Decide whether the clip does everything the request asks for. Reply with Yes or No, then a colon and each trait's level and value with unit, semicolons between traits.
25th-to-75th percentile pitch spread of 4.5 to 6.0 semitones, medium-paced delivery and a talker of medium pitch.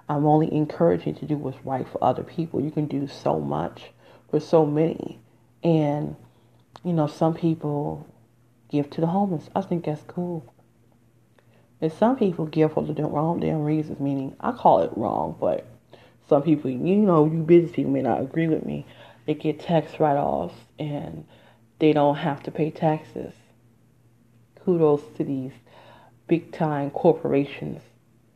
Yes: average, 5.0 semitones; average, 160 wpm; medium, 150 Hz